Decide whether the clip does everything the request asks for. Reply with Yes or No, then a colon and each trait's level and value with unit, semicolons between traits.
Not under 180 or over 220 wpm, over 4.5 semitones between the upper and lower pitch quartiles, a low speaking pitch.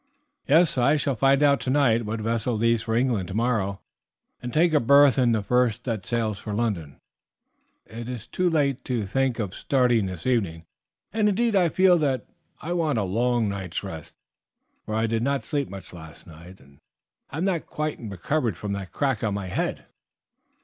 Yes: average, 185 wpm; wide, 5.6 semitones; low, 120 Hz